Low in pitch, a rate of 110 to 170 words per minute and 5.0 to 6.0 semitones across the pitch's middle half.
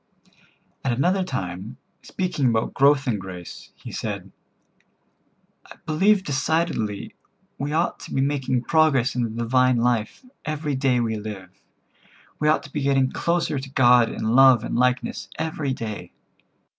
No: low, 130 Hz; average, 145 wpm; average, 4.3 semitones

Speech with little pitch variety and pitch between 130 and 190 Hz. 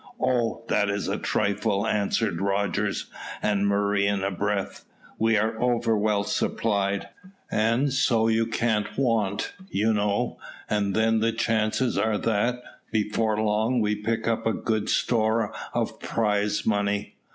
No: narrow, 1.8 semitones; low, 110 Hz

